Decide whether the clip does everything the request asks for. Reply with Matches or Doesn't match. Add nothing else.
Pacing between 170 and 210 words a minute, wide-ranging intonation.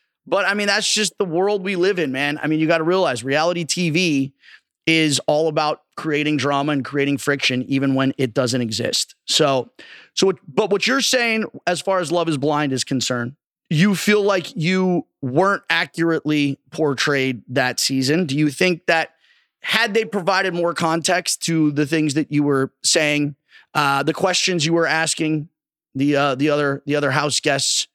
Doesn't match